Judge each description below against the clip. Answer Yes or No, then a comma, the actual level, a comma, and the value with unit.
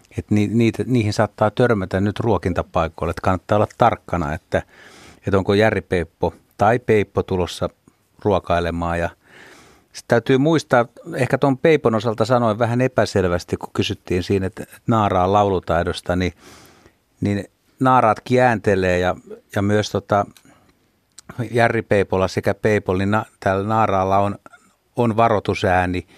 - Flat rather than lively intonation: No, average, 3.8 semitones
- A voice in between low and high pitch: No, low, 105 Hz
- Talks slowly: No, average, 115 wpm